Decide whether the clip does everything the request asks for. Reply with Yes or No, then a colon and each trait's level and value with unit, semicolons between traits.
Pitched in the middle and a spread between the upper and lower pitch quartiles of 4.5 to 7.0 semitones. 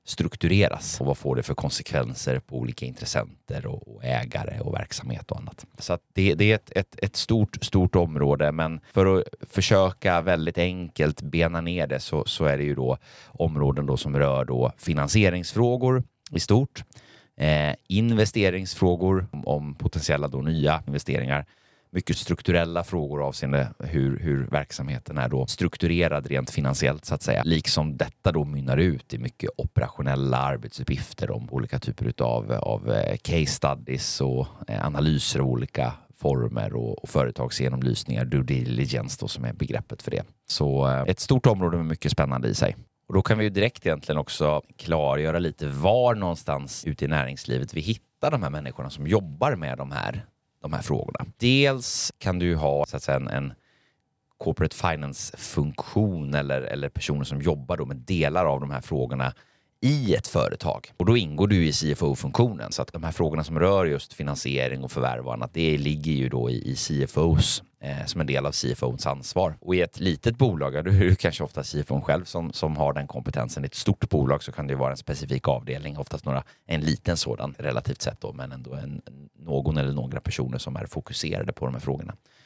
No: very low, 75 Hz; average, 5.2 semitones